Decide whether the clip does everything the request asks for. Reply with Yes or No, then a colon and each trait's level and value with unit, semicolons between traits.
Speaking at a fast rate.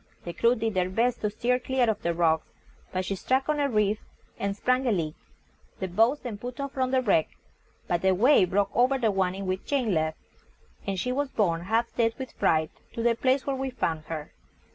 Yes: fast, 225 wpm